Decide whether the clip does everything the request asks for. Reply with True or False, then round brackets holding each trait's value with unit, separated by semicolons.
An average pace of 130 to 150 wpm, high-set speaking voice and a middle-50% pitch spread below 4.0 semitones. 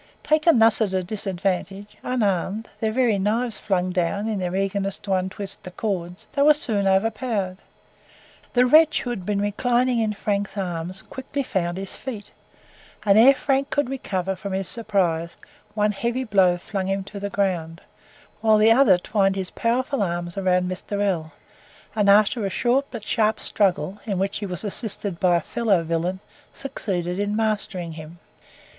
False (165 wpm; 200 Hz; 3.3 semitones)